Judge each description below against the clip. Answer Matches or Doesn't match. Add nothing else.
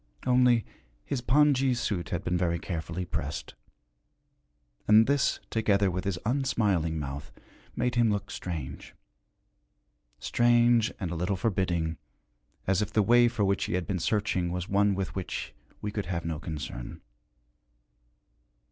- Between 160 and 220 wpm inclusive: Doesn't match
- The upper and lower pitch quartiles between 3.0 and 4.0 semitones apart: Doesn't match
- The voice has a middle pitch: Doesn't match